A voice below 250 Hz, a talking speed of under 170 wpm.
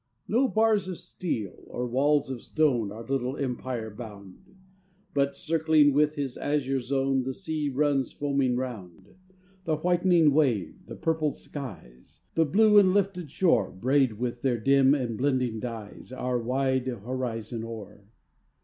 Yes: low, 135 Hz; average, 145 wpm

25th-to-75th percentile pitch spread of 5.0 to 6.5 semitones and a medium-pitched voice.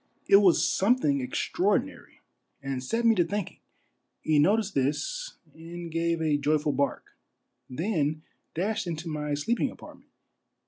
Yes: wide, 5.4 semitones; medium, 165 Hz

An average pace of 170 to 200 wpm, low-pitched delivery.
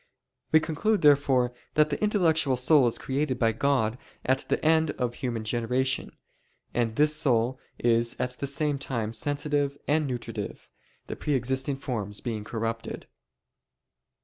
No: average, 145 wpm; low, 130 Hz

